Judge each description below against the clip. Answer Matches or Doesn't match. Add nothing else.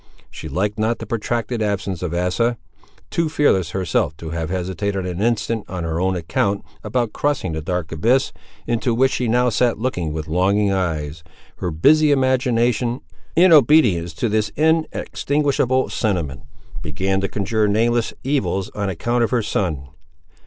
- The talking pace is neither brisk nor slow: Matches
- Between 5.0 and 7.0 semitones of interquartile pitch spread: Matches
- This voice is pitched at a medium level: Doesn't match